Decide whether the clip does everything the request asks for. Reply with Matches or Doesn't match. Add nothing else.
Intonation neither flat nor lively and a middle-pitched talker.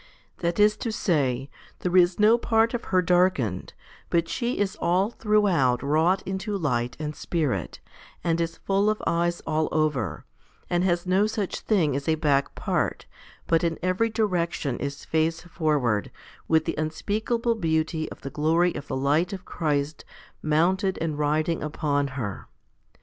Matches